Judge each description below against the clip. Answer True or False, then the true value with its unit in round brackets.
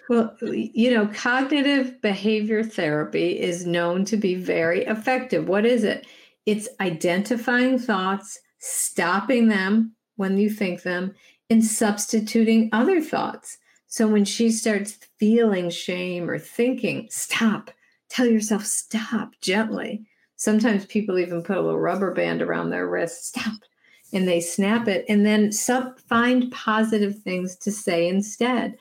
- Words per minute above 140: False (135 wpm)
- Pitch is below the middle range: False (215 Hz)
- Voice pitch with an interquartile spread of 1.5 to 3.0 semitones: False (3.8 semitones)